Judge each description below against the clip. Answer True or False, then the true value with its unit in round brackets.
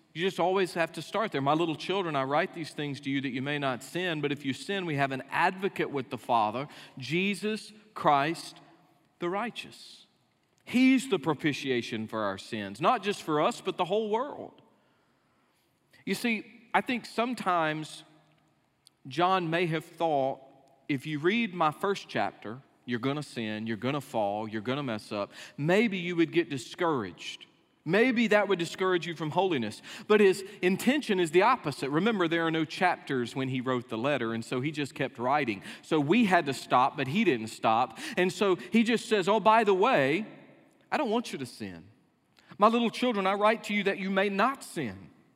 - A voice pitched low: False (170 Hz)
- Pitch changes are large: True (6.4 semitones)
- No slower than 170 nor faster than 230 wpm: True (190 wpm)